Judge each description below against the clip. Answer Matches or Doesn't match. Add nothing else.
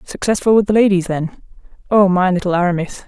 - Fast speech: Doesn't match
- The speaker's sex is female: Matches